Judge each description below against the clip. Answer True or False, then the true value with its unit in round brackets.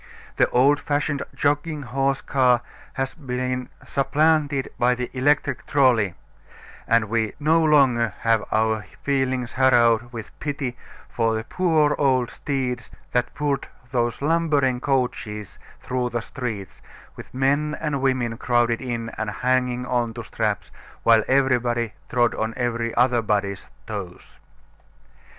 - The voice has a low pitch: True (125 Hz)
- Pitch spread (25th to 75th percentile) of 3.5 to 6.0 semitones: False (2.9 semitones)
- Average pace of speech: False (130 wpm)